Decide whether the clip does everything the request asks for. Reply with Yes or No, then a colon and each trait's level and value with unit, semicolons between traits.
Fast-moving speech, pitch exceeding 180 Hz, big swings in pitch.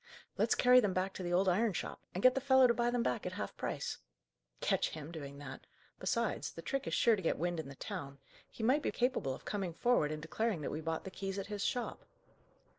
Yes: fast, 245 wpm; high, 190 Hz; wide, 6.8 semitones